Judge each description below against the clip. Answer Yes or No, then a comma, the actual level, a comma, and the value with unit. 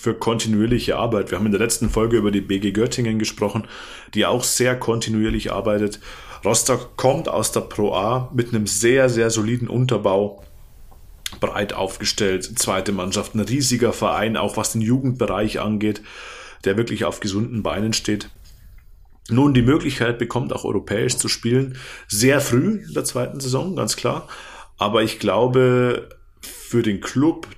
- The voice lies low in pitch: Yes, low, 110 Hz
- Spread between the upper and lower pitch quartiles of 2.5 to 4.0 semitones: Yes, average, 2.8 semitones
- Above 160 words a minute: No, average, 155 wpm